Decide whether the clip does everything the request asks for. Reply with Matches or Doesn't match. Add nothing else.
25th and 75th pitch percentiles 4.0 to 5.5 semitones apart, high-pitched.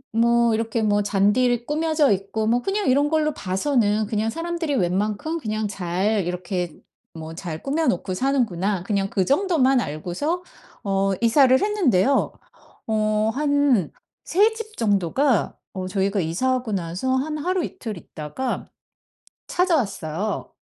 Doesn't match